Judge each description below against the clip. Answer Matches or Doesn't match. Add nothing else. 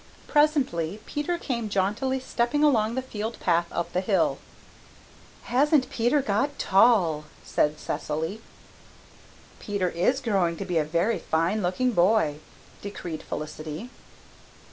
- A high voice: Matches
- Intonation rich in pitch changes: Matches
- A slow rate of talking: Matches